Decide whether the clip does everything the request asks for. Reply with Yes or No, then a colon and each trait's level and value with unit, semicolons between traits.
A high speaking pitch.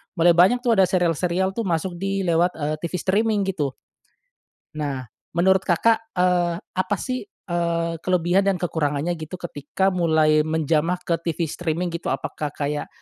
No: medium, 175 Hz